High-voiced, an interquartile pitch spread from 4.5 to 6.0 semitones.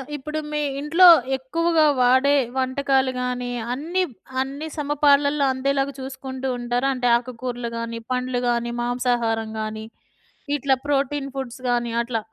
No: very high, 260 Hz; narrow, 2.6 semitones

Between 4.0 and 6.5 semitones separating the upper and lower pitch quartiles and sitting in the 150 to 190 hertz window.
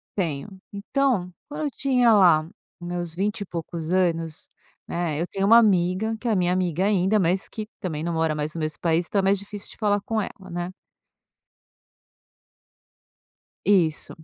No: average, 3.4 semitones; medium, 185 Hz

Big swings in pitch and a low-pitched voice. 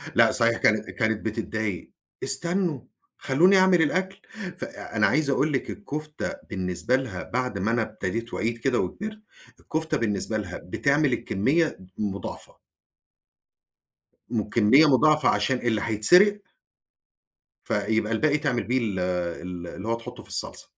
Yes: wide, 6.2 semitones; low, 120 Hz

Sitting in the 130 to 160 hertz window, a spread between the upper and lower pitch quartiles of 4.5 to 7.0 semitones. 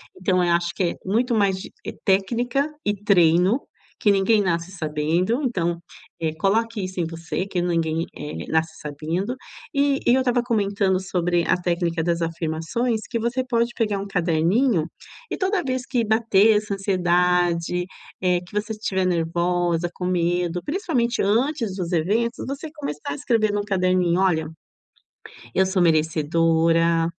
No: medium, 185 Hz; average, 4.8 semitones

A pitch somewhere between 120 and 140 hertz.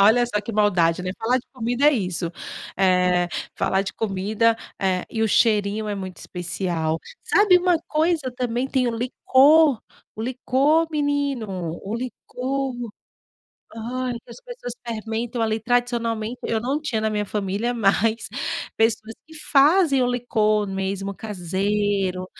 No: high, 225 Hz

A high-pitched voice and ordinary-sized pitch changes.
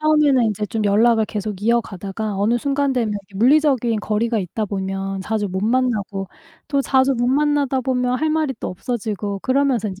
Yes: high, 230 Hz; average, 4.4 semitones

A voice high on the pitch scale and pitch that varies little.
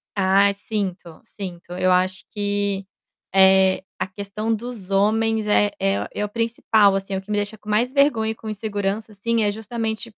Yes: high, 205 Hz; narrow, 2.3 semitones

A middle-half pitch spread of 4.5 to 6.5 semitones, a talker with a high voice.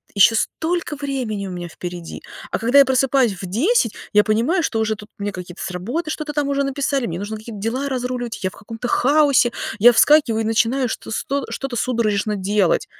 Yes: average, 4.9 semitones; high, 235 Hz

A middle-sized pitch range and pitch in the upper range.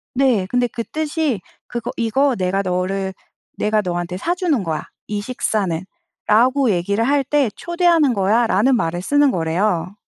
No: wide, 6.5 semitones; high, 220 Hz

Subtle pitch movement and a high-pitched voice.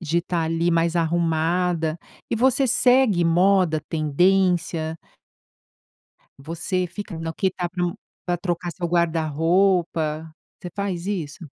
No: narrow, 2.1 semitones; medium, 170 Hz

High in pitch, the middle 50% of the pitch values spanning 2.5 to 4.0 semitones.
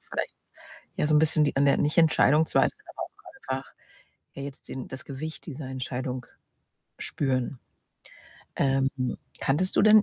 No: medium, 140 Hz; average, 2.9 semitones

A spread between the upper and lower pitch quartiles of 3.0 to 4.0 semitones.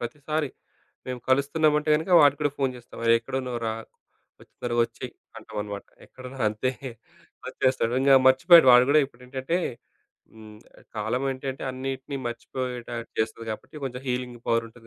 No: narrow, 2.6 semitones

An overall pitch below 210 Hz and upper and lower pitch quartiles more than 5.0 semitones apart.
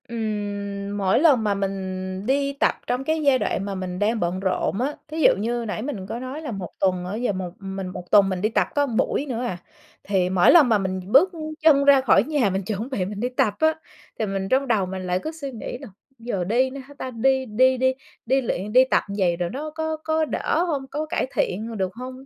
No: high, 230 Hz; wide, 5.6 semitones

